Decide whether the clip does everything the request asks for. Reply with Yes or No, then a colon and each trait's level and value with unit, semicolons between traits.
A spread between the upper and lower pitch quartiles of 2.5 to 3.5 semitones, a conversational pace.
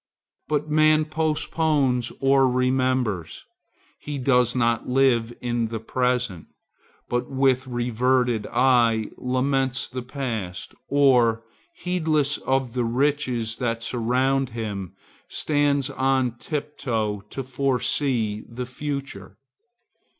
No: average, 2.8 semitones; slow, 100 wpm